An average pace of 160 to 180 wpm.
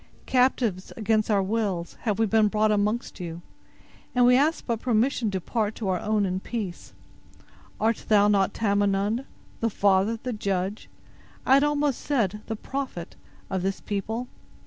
No: average, 150 wpm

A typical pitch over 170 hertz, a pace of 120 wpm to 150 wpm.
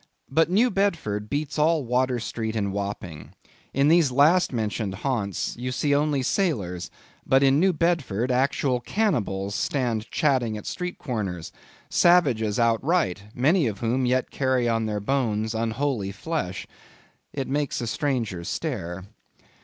No: low, 125 Hz; average, 140 wpm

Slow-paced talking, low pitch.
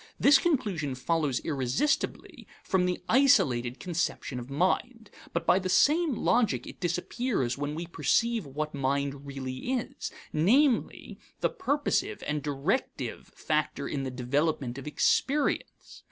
No: slow, 130 wpm; medium, 165 Hz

